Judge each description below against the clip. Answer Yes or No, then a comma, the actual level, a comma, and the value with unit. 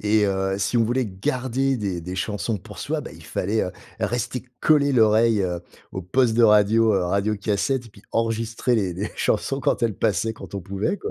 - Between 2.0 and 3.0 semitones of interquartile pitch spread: No, average, 3.4 semitones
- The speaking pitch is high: No, low, 110 Hz